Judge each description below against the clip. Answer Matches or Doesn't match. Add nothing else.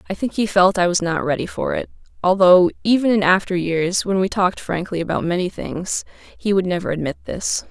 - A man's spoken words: Doesn't match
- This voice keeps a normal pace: Doesn't match